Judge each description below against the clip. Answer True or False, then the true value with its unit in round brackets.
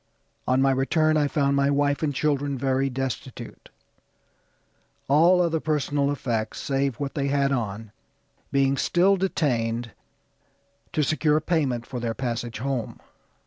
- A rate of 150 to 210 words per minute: False (135 wpm)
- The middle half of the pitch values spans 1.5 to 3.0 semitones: True (2.7 semitones)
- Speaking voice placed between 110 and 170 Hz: True (140 Hz)